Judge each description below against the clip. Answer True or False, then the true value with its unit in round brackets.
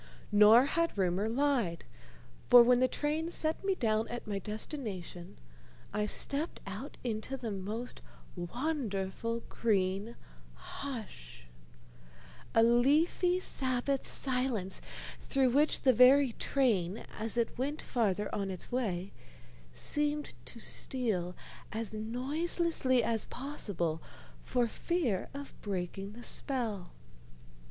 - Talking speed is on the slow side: True (115 wpm)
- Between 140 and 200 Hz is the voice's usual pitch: False (235 Hz)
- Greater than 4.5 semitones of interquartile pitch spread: True (5.1 semitones)